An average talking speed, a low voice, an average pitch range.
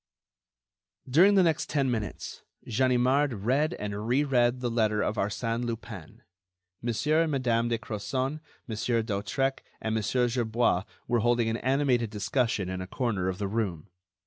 Yes: average, 150 wpm; low, 120 Hz; average, 3.4 semitones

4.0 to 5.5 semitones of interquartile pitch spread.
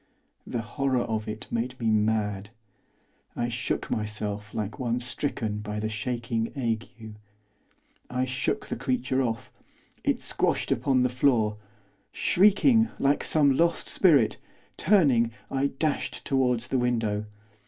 No: average, 3.6 semitones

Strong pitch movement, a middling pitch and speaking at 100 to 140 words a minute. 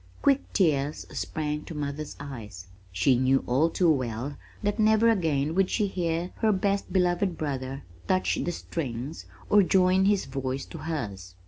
No: wide, 5.7 semitones; medium, 155 Hz; average, 155 wpm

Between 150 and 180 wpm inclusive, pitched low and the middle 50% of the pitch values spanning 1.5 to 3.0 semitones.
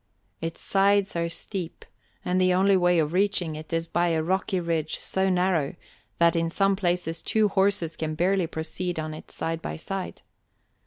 No: average, 175 wpm; medium, 175 Hz; narrow, 2.6 semitones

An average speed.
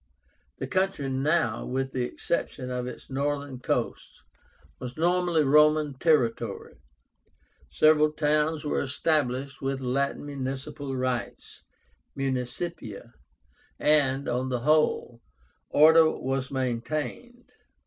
No: slow, 100 wpm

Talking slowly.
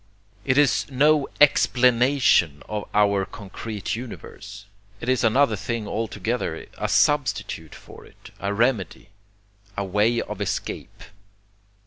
Yes: slow, 115 wpm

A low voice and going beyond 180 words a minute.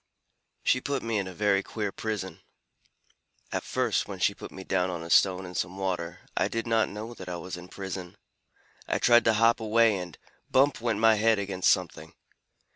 Yes: low, 100 Hz; average, 200 wpm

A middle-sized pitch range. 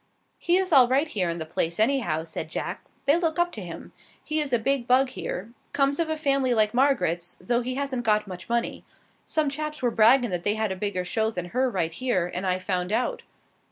No: wide, 7.1 semitones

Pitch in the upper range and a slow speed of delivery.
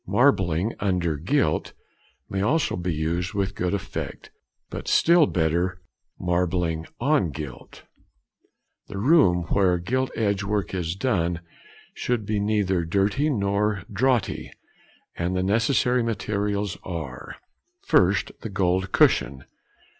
No: very low, 95 Hz; slow, 115 wpm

